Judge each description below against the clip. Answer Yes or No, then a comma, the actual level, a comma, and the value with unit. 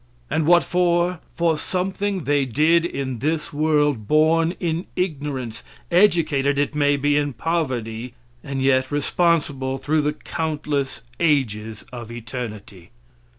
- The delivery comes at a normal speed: No, slow, 125 wpm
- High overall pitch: No, medium, 145 Hz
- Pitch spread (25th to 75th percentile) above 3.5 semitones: Yes, average, 3.9 semitones